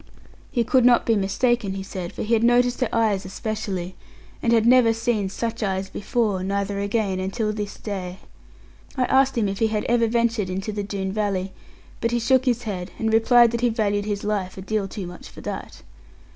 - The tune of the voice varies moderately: Yes, average, 3.2 semitones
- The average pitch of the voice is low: No, high, 215 Hz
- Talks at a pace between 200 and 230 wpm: Yes, fast, 205 wpm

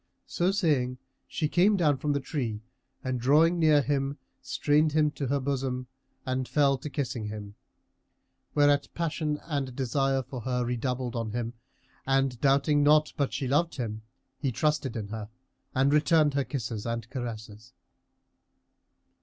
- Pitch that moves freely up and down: No, average, 3.3 semitones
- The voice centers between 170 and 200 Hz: No, low, 135 Hz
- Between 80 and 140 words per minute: No, average, 150 wpm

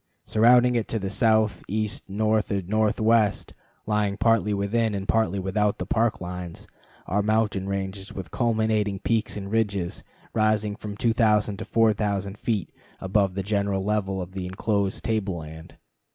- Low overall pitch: Yes, low, 105 Hz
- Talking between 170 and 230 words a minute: No, average, 150 wpm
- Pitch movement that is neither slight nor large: No, narrow, 2.1 semitones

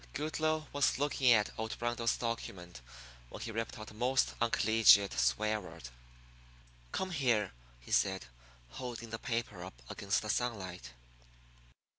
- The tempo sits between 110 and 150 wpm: Yes, slow, 135 wpm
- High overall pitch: No, low, 115 Hz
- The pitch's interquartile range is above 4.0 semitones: No, average, 3.7 semitones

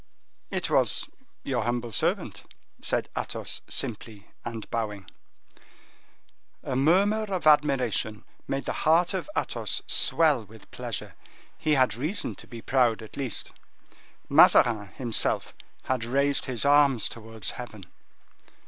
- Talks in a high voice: No, low, 125 Hz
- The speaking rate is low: Yes, slow, 120 wpm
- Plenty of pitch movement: No, average, 4.3 semitones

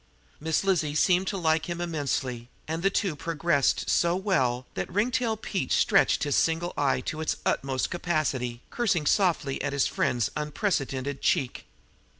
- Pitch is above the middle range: No, medium, 155 Hz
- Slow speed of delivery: No, average, 150 wpm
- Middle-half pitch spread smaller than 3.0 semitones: No, average, 4.5 semitones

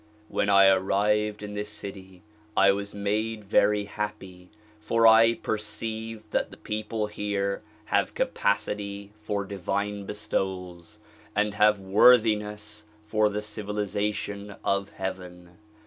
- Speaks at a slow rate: Yes, slow, 115 wpm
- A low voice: Yes, low, 105 Hz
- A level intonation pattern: Yes, narrow, 1.3 semitones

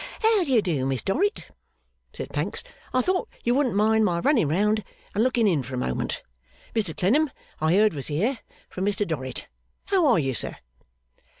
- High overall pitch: Yes, high, 210 Hz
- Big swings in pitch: Yes, wide, 8.1 semitones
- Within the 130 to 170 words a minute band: No, average, 180 wpm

